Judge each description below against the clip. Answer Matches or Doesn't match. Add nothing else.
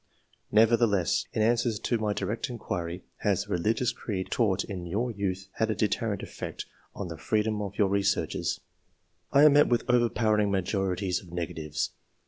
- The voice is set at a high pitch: Doesn't match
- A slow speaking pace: Doesn't match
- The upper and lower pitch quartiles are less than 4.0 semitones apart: Matches